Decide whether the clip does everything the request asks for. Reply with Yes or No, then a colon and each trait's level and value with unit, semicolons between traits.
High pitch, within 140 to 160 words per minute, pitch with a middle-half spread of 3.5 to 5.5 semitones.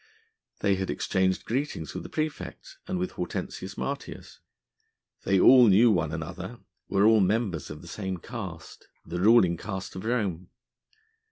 No: very low, 95 Hz; average, 150 wpm; average, 3.9 semitones